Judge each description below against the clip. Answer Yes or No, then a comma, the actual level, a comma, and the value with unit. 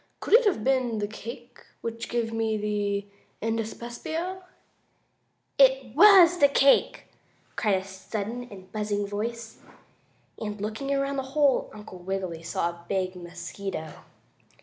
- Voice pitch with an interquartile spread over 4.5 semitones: Yes, average, 4.9 semitones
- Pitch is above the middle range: Yes, high, 220 Hz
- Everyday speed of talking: No, slow, 130 wpm